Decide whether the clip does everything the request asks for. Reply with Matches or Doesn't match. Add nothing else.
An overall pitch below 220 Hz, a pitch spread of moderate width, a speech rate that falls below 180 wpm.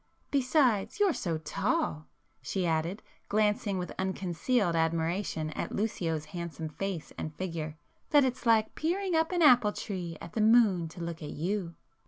Doesn't match